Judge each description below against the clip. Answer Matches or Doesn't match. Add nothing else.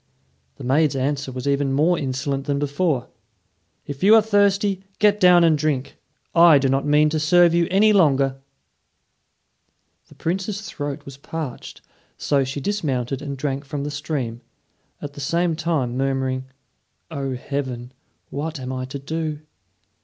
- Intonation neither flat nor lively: Matches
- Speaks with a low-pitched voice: Doesn't match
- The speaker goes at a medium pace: Matches